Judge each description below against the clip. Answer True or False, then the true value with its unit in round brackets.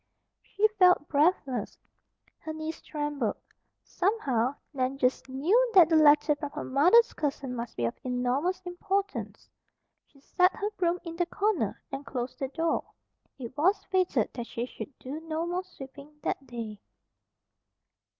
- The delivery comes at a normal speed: True (150 wpm)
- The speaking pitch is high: True (295 Hz)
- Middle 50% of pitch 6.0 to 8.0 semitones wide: False (5.5 semitones)